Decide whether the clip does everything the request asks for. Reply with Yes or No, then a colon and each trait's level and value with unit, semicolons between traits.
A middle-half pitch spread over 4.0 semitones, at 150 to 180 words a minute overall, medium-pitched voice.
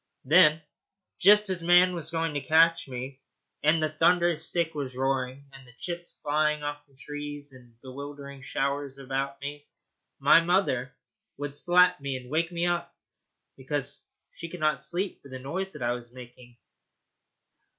No: average, 3.7 semitones; average, 160 wpm; medium, 145 Hz